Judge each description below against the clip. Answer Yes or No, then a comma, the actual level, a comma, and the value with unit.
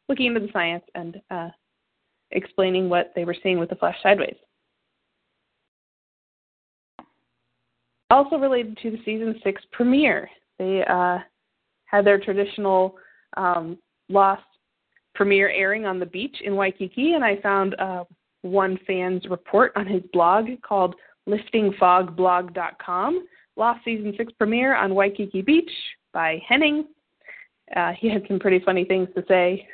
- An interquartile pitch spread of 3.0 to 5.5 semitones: Yes, average, 3.6 semitones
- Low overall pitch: No, high, 195 Hz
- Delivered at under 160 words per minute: Yes, slow, 135 wpm